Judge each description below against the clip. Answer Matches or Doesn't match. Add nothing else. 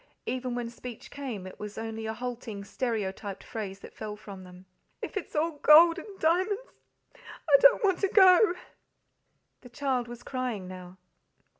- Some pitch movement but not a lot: Doesn't match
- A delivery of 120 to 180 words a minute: Matches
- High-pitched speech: Matches